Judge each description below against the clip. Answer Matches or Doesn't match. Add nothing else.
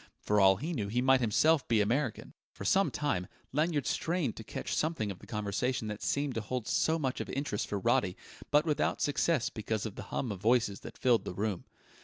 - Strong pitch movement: Matches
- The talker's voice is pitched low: Matches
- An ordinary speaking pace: Doesn't match